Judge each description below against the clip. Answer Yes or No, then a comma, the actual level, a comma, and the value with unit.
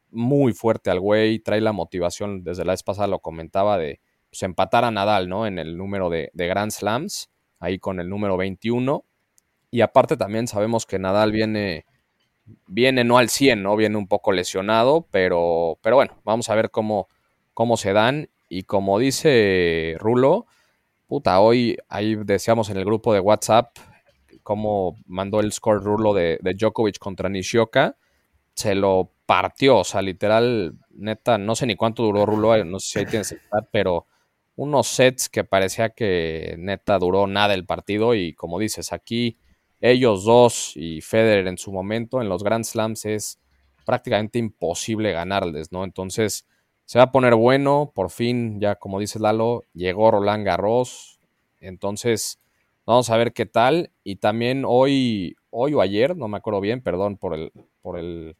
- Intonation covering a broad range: No, average, 3.3 semitones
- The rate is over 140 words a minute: Yes, average, 170 wpm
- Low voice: Yes, low, 105 Hz